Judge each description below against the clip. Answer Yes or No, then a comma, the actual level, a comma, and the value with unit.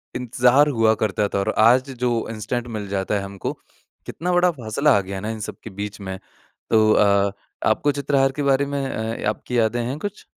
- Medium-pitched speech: No, low, 115 Hz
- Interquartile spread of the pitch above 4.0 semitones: Yes, average, 4.6 semitones